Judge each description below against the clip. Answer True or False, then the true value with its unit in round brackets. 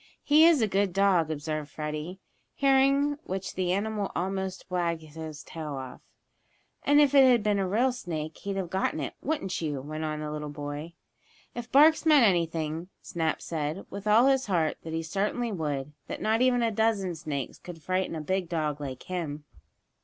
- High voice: False (180 Hz)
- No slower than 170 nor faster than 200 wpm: True (185 wpm)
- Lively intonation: True (6.0 semitones)